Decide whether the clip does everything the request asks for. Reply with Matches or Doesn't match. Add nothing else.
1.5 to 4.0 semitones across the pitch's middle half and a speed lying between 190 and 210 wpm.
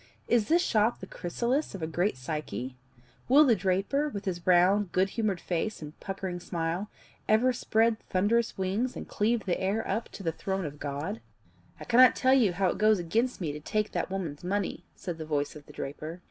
Doesn't match